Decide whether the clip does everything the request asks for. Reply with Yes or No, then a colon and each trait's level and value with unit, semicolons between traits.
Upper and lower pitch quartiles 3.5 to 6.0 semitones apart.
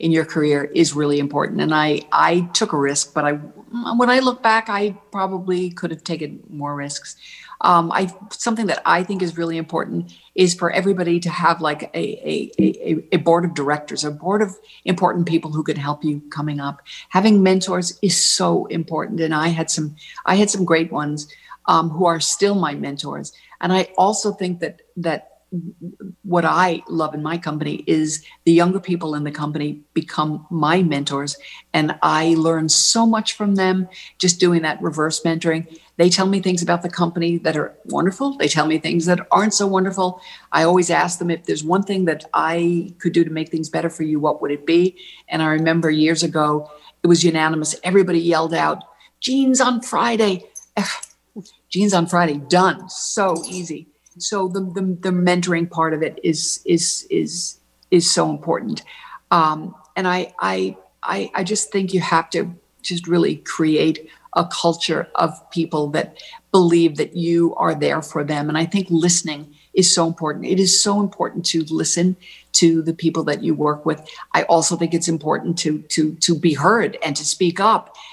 No: average, 3.1 semitones